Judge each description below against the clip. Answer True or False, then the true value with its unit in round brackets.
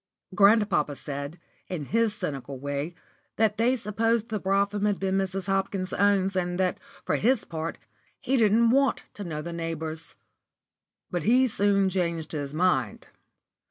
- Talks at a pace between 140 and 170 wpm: True (145 wpm)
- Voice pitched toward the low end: False (190 Hz)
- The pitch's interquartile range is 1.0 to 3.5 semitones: False (4.2 semitones)